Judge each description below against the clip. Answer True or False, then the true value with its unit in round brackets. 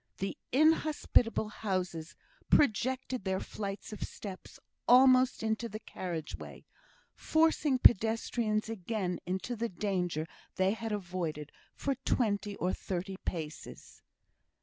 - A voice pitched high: True (210 Hz)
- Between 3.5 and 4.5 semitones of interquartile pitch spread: True (4.2 semitones)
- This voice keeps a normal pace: False (110 wpm)